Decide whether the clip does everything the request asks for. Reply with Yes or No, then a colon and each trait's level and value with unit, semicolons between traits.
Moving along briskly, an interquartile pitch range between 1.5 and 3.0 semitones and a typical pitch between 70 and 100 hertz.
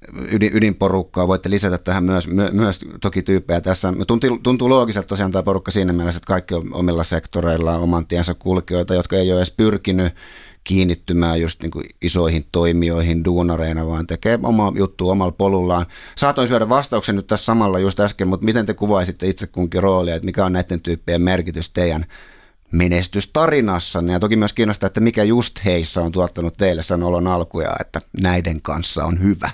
Yes: fast, 175 wpm; average, 2.7 semitones; very low, 90 Hz